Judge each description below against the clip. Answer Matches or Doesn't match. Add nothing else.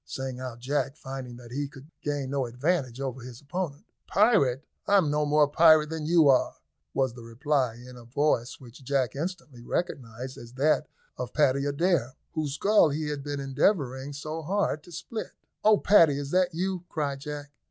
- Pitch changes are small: Doesn't match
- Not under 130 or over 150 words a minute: Doesn't match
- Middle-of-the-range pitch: Matches